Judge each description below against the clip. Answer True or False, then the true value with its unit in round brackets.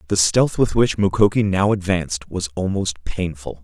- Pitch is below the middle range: True (95 Hz)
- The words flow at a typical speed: True (165 wpm)